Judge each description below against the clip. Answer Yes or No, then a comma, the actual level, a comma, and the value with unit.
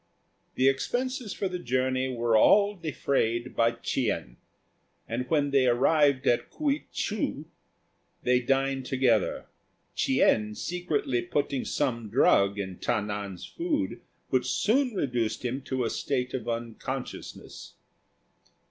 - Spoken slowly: Yes, slow, 120 wpm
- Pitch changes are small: No, average, 4.0 semitones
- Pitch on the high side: No, low, 130 Hz